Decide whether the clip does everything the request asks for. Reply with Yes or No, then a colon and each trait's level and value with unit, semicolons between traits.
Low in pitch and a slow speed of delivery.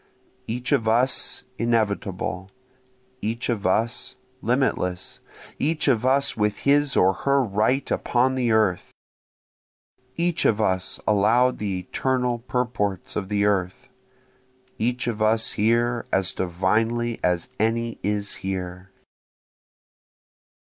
Yes: low, 110 Hz; slow, 115 wpm